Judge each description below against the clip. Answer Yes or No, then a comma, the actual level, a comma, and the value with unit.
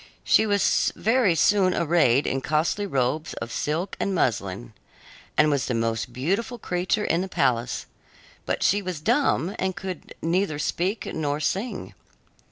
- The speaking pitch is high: No, medium, 170 Hz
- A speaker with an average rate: Yes, average, 150 wpm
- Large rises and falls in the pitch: Yes, wide, 5.9 semitones